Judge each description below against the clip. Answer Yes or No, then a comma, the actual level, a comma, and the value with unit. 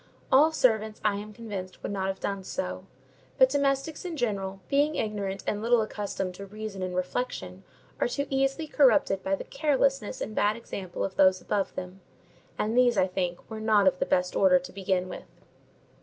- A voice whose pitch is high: Yes, high, 205 Hz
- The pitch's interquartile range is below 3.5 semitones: No, average, 4.6 semitones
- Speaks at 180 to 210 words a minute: Yes, average, 185 wpm